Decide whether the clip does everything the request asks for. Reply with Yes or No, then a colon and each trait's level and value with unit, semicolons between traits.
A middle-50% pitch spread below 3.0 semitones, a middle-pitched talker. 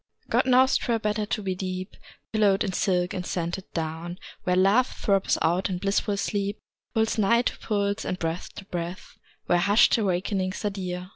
No: narrow, 2.5 semitones; high, 195 Hz